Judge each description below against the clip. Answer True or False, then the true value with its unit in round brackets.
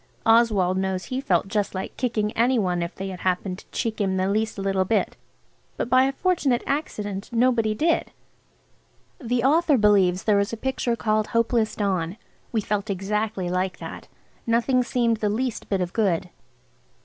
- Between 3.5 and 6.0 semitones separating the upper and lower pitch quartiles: True (3.9 semitones)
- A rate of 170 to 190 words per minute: True (175 wpm)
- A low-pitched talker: False (215 Hz)